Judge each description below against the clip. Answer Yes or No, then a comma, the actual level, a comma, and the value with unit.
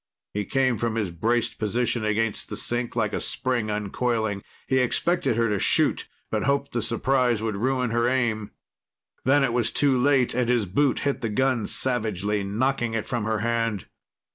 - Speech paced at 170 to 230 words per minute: Yes, average, 180 wpm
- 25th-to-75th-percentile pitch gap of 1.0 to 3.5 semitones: Yes, average, 2.9 semitones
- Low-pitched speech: Yes, low, 115 Hz